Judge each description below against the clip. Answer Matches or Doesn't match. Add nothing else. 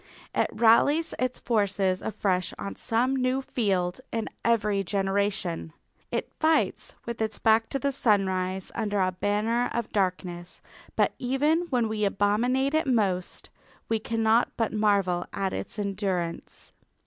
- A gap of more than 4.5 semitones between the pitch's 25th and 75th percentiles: Doesn't match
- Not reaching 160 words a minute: Matches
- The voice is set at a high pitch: Matches